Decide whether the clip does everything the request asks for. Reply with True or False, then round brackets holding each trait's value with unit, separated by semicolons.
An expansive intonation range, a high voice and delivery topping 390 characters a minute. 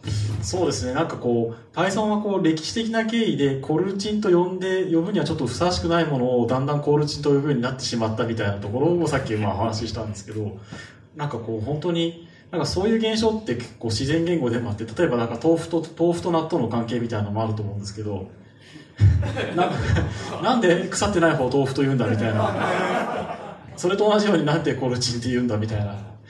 False (6.9 semitones; 130 Hz; 465 characters per minute)